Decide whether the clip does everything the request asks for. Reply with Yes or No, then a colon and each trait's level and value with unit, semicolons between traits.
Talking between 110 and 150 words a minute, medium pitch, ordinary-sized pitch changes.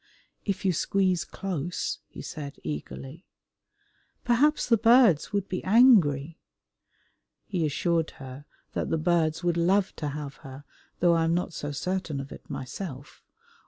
Yes: average, 145 wpm; medium, 170 Hz; average, 4.6 semitones